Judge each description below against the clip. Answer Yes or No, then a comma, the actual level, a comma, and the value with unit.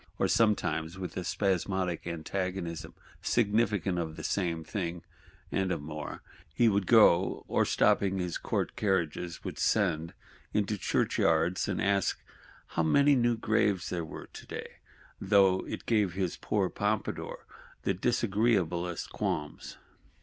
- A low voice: Yes, very low, 95 Hz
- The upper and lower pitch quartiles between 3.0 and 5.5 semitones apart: Yes, average, 3.4 semitones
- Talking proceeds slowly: Yes, slow, 130 wpm